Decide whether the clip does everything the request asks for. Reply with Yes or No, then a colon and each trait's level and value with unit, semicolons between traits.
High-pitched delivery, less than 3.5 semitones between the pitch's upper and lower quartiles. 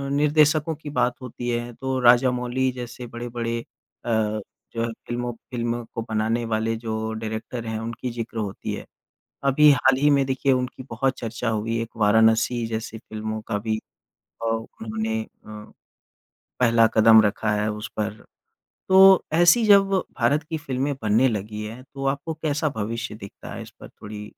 No: low, 115 Hz; average, 2.9 semitones